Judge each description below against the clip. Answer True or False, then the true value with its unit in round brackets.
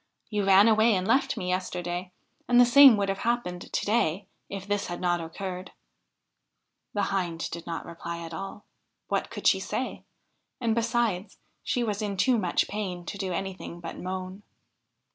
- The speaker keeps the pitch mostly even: False (3.3 semitones)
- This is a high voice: True (195 Hz)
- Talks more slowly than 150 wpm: False (175 wpm)